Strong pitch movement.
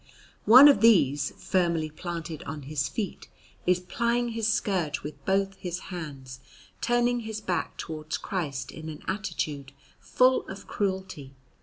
Yes: wide, 5.7 semitones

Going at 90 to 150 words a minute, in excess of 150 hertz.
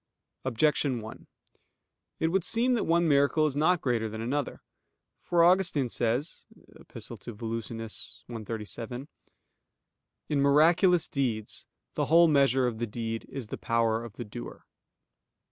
No: slow, 135 wpm; low, 130 Hz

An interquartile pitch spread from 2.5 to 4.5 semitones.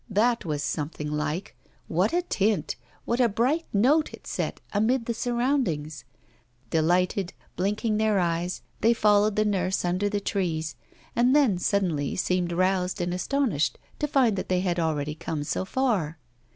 No: average, 5.1 semitones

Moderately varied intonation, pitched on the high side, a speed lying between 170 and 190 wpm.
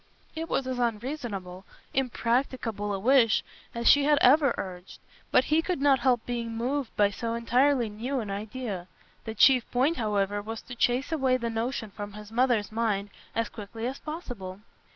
Yes: average, 3.9 semitones; high, 235 Hz; average, 175 wpm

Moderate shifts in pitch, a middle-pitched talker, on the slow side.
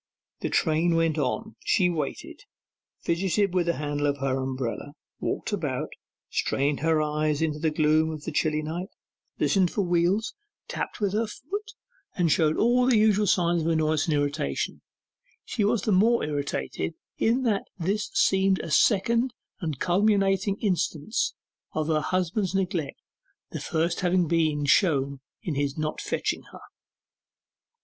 No: average, 4.5 semitones; medium, 170 Hz; average, 150 wpm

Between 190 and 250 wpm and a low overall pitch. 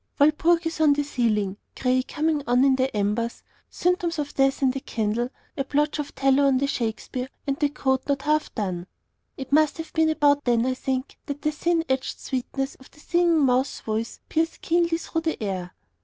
No: average, 195 wpm; very high, 275 Hz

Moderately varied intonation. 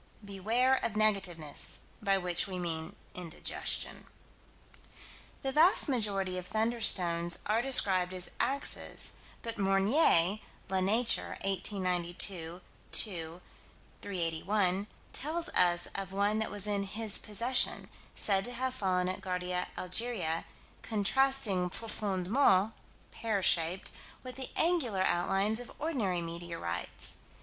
Yes: average, 3.9 semitones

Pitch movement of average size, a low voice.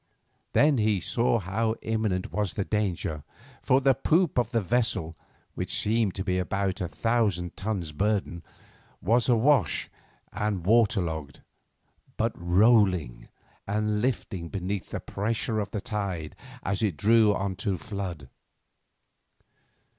Yes: average, 3.6 semitones; low, 105 Hz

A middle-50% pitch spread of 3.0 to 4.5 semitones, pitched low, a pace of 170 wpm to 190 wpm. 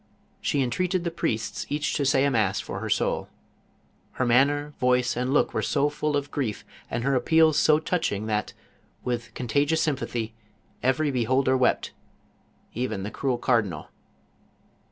No: average, 3.6 semitones; low, 130 Hz; average, 155 wpm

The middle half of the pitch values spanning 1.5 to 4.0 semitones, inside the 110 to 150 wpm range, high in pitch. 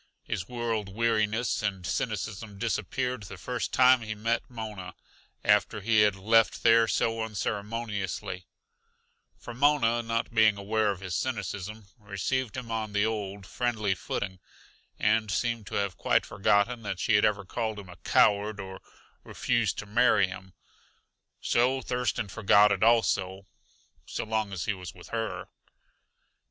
No: narrow, 2.5 semitones; average, 145 wpm; low, 110 Hz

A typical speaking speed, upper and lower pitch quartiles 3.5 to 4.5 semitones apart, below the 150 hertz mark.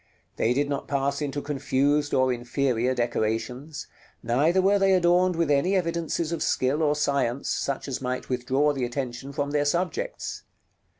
Yes: average, 160 wpm; average, 3.8 semitones; medium, 140 Hz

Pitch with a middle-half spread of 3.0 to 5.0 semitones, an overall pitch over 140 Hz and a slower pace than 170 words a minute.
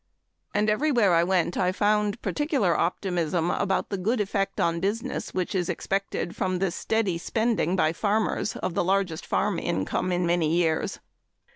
Yes: average, 3.3 semitones; high, 190 Hz; average, 160 wpm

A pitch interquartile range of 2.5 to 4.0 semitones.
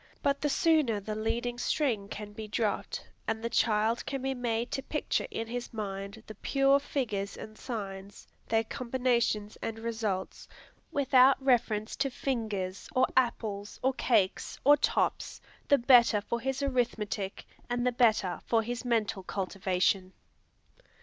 Yes: average, 3.5 semitones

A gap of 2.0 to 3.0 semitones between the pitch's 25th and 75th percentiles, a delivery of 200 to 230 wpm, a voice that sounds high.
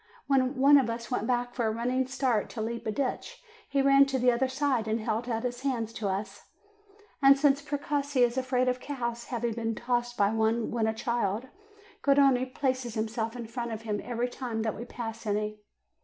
Yes: narrow, 2.6 semitones; fast, 205 wpm; high, 240 Hz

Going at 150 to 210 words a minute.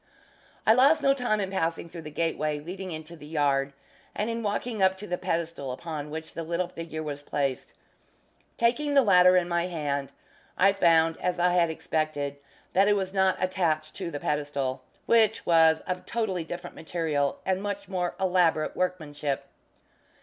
Yes: average, 170 wpm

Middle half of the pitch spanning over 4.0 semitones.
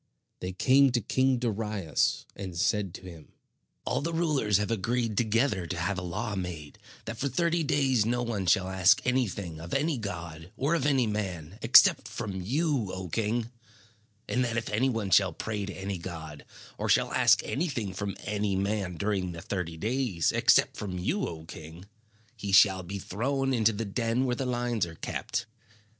Yes: average, 4.9 semitones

